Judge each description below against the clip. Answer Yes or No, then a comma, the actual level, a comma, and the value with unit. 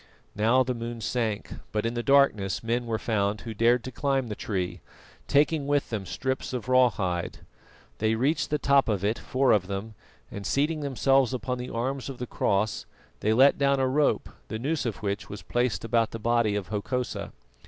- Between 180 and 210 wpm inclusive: Yes, average, 195 wpm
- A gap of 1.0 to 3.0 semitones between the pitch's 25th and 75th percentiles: No, average, 3.7 semitones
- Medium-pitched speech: No, low, 120 Hz